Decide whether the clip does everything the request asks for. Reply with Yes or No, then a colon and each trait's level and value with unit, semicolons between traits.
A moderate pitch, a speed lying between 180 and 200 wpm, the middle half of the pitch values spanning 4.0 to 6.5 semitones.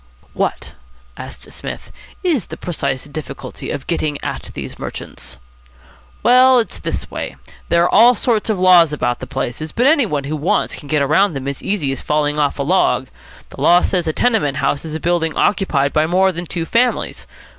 Yes: medium, 160 Hz; average, 190 wpm; average, 5.3 semitones